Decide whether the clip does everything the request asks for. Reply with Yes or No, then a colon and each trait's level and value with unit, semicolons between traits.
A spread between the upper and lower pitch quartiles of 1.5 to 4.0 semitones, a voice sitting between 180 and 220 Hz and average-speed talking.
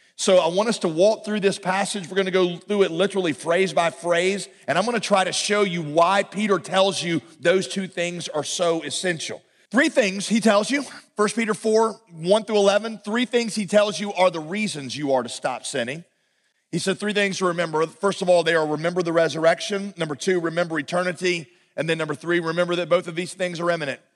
No: average, 3.2 semitones; medium, 185 Hz; fast, 225 wpm